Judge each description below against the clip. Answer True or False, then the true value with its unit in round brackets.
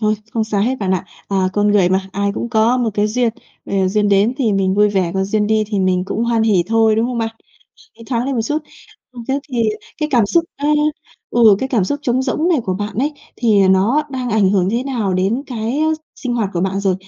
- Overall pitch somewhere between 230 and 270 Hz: False (220 Hz)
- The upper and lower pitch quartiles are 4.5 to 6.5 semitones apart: False (3.7 semitones)